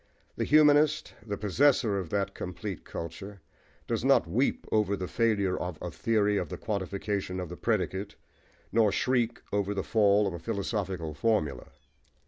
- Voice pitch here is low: Yes, low, 100 Hz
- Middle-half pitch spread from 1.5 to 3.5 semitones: Yes, average, 3.2 semitones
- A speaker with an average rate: Yes, average, 155 wpm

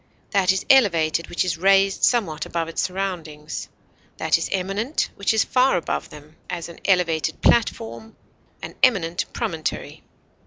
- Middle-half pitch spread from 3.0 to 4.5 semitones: Yes, average, 3.6 semitones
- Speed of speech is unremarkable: Yes, average, 145 wpm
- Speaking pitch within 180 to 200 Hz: Yes, medium, 185 Hz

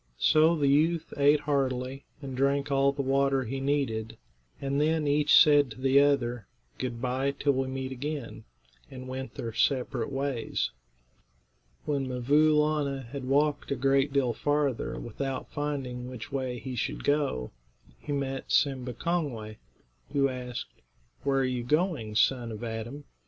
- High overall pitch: No, low, 135 Hz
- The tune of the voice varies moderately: No, narrow, 2.2 semitones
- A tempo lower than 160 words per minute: Yes, average, 150 wpm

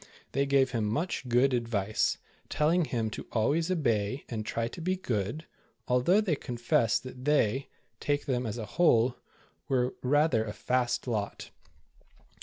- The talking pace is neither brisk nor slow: Yes, average, 150 wpm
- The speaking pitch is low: Yes, low, 125 Hz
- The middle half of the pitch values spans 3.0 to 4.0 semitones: No, average, 4.4 semitones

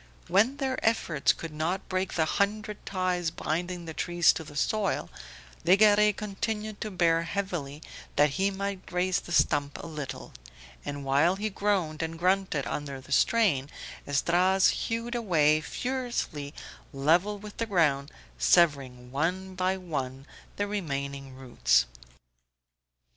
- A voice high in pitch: No, medium, 175 Hz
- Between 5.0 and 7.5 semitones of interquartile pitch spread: Yes, wide, 5.5 semitones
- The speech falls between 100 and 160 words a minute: Yes, slow, 135 wpm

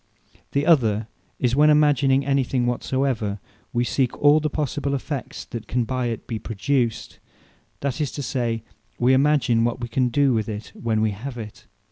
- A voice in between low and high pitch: No, low, 125 Hz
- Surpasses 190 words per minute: No, average, 180 wpm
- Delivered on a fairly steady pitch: No, average, 3.4 semitones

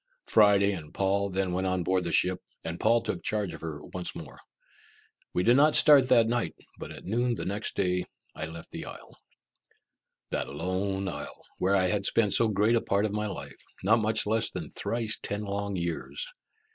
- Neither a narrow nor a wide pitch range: Yes, average, 3.2 semitones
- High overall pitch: No, low, 100 Hz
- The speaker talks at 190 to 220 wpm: Yes, average, 195 wpm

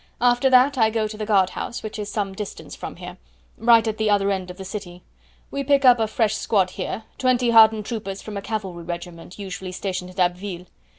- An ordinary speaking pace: No, fast, 220 wpm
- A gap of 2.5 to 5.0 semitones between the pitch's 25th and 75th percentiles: Yes, average, 3.3 semitones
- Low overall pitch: No, high, 210 Hz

